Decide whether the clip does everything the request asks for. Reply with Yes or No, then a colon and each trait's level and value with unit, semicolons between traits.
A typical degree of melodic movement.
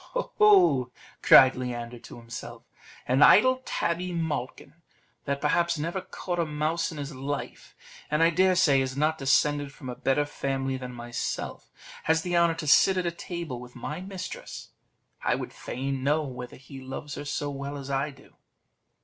Yes: average, 4.3 semitones